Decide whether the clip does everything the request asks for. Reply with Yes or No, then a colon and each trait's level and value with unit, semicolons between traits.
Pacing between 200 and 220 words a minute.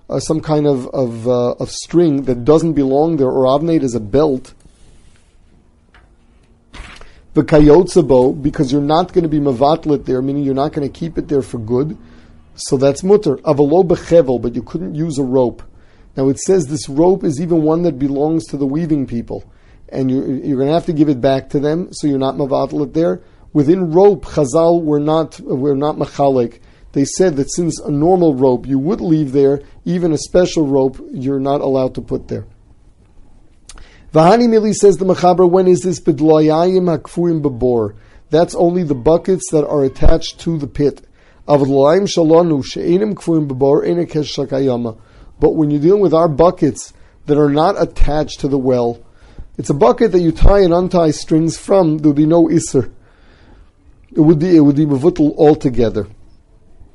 No: average, 170 wpm